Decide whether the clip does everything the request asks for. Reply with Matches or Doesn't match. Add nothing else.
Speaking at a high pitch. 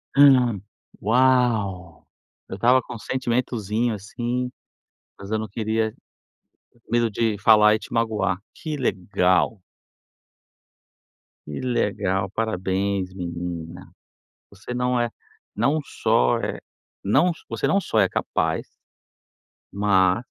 Doesn't match